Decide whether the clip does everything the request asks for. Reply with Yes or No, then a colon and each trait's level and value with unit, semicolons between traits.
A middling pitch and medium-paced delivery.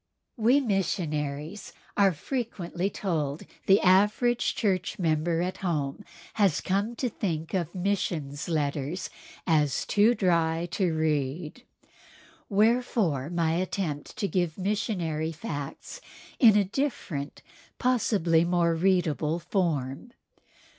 No: medium, 175 Hz; slow, 110 wpm